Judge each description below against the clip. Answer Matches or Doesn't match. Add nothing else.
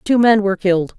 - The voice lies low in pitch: Doesn't match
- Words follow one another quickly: Matches